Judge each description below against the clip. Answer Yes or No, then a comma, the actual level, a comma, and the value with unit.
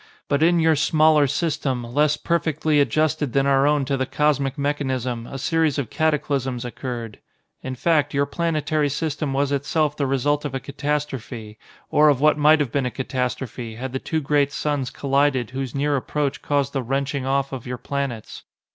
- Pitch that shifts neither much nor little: No, narrow, 2.2 semitones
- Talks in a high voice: No, medium, 140 Hz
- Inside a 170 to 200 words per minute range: Yes, average, 180 wpm